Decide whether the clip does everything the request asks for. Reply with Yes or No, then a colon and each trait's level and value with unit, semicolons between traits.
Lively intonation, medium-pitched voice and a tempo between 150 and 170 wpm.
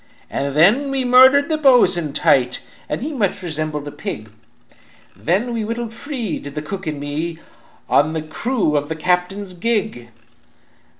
Yes: wide, 7.9 semitones; medium, 180 Hz; average, 155 wpm